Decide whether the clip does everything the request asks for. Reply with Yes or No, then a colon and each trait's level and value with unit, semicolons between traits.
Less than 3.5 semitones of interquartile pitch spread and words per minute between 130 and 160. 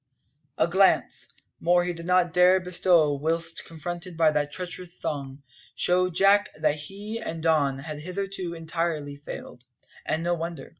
Yes: average, 2.8 semitones; average, 150 wpm